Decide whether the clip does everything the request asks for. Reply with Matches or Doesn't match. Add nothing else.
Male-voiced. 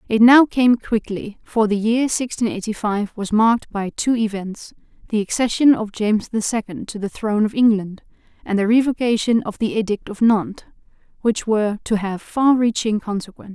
Doesn't match